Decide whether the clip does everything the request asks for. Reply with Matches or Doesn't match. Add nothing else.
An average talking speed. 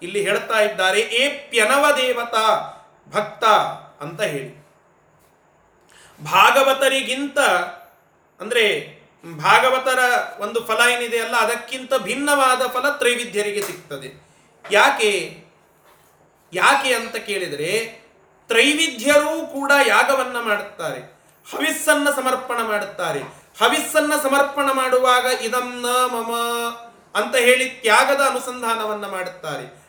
Matches